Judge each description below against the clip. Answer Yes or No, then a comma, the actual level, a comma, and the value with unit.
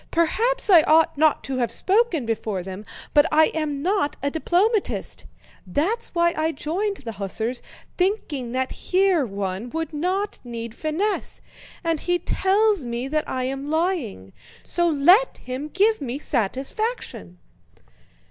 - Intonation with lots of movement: Yes, wide, 6.8 semitones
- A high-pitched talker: Yes, very high, 310 Hz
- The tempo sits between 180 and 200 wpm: No, average, 140 wpm